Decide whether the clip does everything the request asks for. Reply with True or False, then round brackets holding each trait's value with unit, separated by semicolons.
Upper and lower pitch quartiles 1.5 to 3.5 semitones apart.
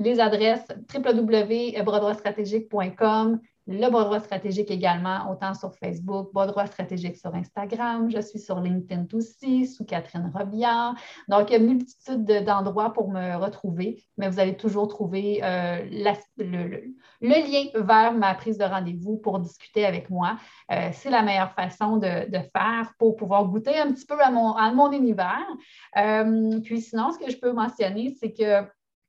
True (2.8 semitones)